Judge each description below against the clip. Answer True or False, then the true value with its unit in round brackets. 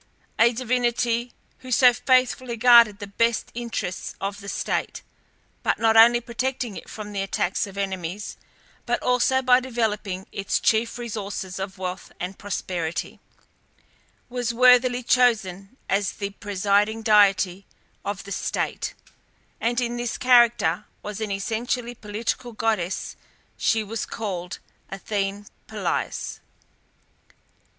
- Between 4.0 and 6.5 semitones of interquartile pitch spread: False (3.3 semitones)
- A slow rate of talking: True (125 wpm)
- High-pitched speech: True (220 Hz)